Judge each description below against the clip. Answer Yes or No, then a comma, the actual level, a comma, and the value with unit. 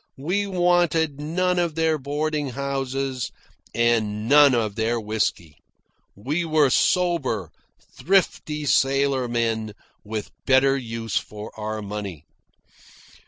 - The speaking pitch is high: No, low, 135 Hz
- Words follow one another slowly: Yes, slow, 105 wpm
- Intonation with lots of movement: Yes, wide, 5.8 semitones